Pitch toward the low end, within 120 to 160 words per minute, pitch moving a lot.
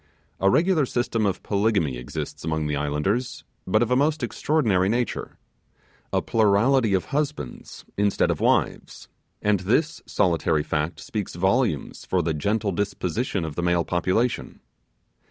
Yes: low, 100 Hz; average, 140 wpm; wide, 5.8 semitones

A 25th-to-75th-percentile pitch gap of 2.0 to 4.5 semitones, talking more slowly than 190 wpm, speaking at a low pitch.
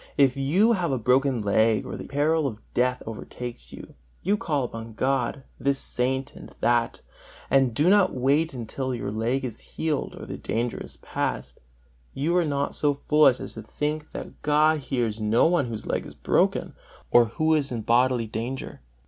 Yes: average, 4.0 semitones; average, 180 wpm; low, 130 Hz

